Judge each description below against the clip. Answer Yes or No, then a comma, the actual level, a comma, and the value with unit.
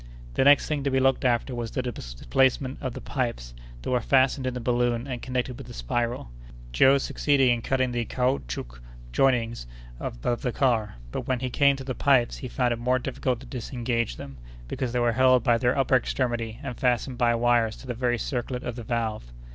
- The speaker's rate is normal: No, fast, 210 wpm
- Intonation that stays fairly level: Yes, narrow, 1.9 semitones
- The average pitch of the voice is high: No, low, 125 Hz